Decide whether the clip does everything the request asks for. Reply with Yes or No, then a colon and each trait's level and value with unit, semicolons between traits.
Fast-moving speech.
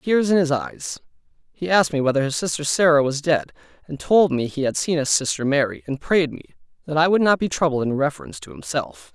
Yes: fast, 235 wpm